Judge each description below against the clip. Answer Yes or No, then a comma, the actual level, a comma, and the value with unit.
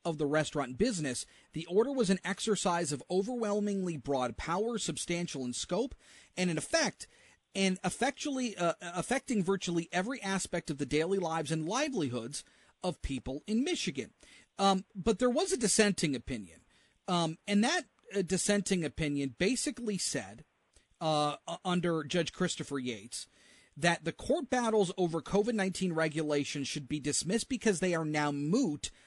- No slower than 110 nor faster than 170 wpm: Yes, average, 150 wpm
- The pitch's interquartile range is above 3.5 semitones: Yes, average, 5.2 semitones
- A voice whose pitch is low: No, medium, 180 Hz